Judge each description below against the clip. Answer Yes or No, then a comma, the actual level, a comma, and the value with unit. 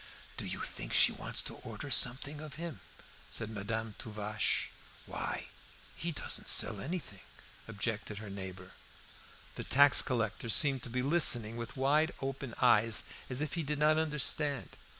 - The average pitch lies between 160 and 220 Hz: No, low, 125 Hz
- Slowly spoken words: No, average, 150 wpm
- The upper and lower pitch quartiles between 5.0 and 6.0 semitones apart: Yes, wide, 5.5 semitones